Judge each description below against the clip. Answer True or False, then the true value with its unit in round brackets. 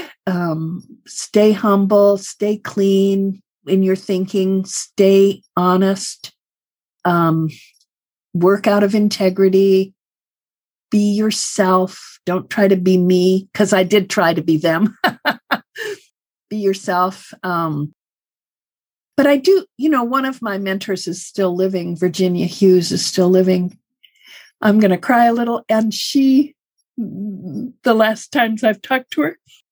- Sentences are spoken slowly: True (125 wpm)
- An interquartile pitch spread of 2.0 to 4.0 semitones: True (2.9 semitones)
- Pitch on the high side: True (195 Hz)